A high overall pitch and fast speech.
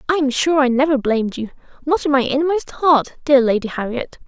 Yes: very high, 275 Hz; fast, 210 wpm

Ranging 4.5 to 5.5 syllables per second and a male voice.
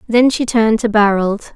No: 5.1 syllables/s; female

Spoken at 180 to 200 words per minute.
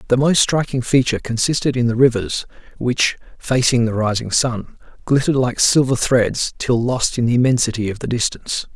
No: average, 170 wpm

